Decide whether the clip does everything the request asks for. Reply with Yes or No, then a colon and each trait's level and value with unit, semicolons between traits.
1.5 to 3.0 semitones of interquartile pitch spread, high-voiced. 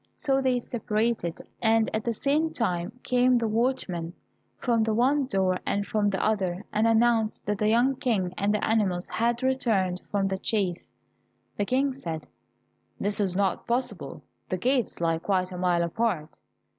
No: average, 4.3 semitones; high, 215 Hz